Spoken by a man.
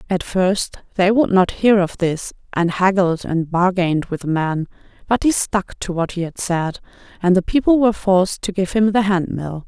No: female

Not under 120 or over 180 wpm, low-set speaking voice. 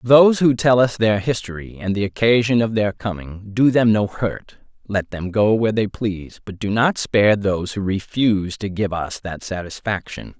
No: average, 195 wpm; low, 105 Hz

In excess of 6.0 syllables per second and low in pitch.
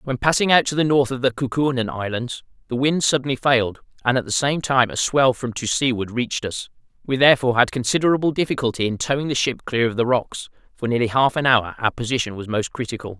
Yes: 6.2 syllables/s; low, 125 Hz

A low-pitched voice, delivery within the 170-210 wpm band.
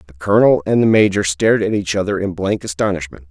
No: very low, 95 Hz; fast, 220 wpm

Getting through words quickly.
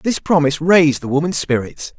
No: average, 180 wpm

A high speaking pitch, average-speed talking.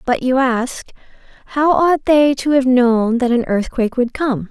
Yes: very high, 255 Hz; average, 185 wpm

